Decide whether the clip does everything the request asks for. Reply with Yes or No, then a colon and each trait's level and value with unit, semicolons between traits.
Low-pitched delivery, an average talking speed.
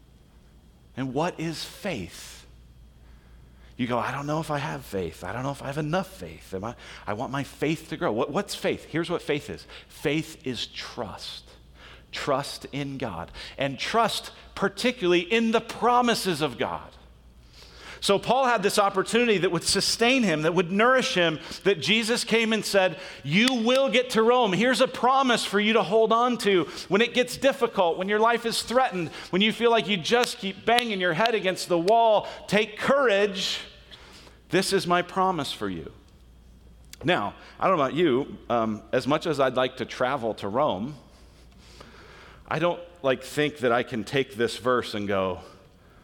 No: medium, 165 Hz; average, 180 wpm